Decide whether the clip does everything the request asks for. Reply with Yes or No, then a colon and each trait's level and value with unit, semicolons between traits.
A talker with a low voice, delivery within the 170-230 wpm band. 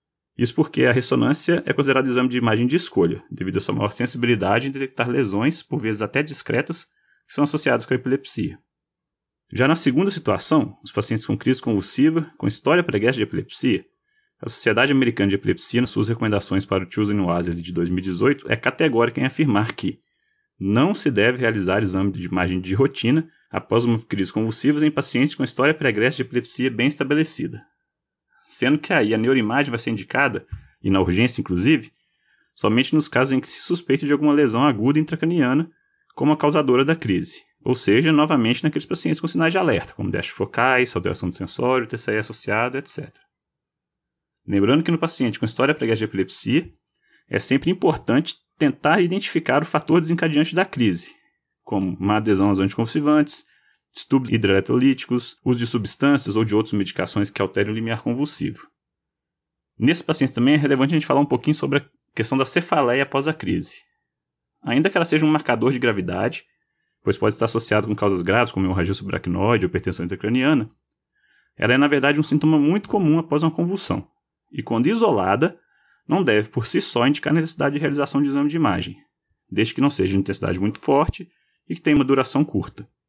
Yes: low, 125 Hz; average, 180 wpm